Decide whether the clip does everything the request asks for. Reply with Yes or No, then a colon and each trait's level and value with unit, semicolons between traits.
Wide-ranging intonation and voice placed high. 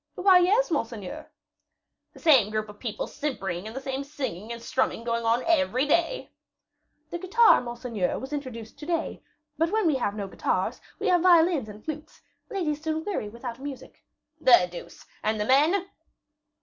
Yes: wide, 6.3 semitones; very high, 270 Hz